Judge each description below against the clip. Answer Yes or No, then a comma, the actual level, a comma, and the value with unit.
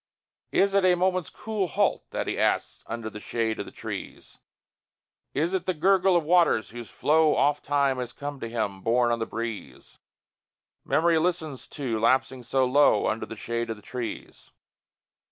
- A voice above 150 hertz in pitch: No, medium, 140 Hz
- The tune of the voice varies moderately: No, wide, 6.6 semitones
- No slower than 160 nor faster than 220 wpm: Yes, average, 170 wpm